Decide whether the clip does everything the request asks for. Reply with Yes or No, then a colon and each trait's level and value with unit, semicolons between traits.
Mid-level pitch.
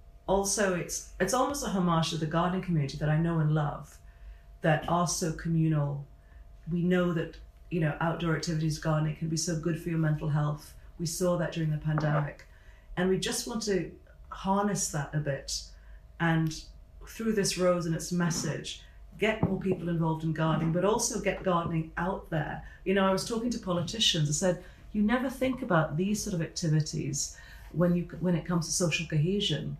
Yes: medium, 165 Hz